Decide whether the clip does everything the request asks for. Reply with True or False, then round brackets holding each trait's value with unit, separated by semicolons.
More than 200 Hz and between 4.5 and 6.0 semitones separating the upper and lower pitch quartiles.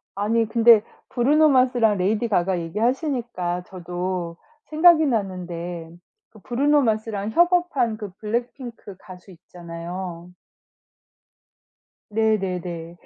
True (210 Hz; 5.2 semitones)